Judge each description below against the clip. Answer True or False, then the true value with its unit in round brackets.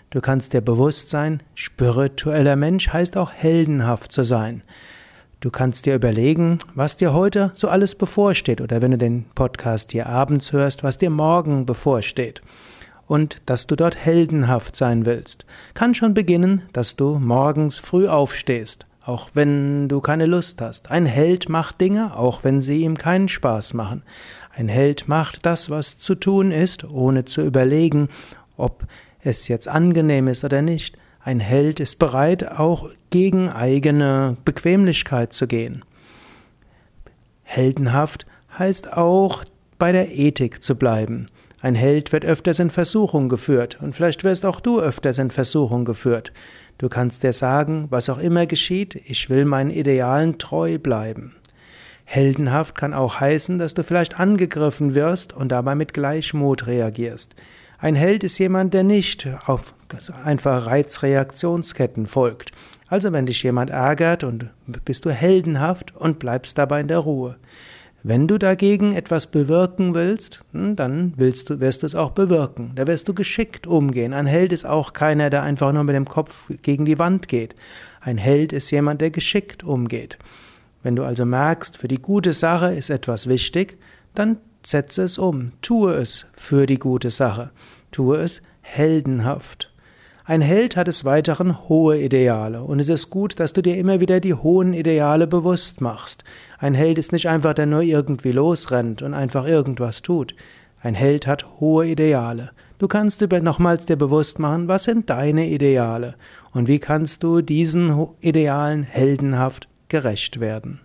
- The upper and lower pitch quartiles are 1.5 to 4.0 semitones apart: False (4.7 semitones)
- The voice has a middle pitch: True (145 Hz)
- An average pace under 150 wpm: False (160 wpm)